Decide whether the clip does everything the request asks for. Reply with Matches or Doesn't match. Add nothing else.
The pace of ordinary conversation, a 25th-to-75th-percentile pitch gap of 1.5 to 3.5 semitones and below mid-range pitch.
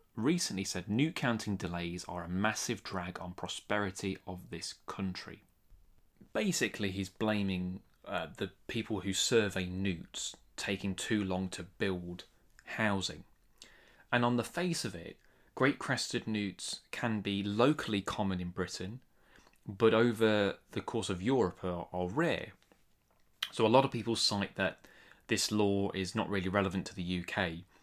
Matches